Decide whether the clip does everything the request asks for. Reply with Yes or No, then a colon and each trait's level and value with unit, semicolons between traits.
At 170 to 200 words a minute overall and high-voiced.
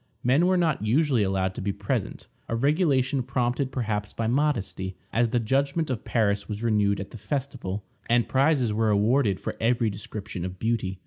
No: average, 180 wpm; low, 115 Hz